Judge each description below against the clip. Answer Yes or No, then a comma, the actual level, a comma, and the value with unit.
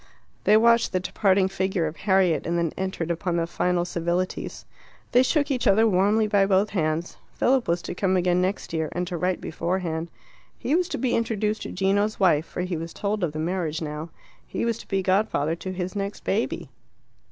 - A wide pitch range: No, average, 3.3 semitones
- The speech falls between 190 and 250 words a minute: Yes, average, 200 wpm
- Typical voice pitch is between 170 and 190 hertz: Yes, medium, 185 Hz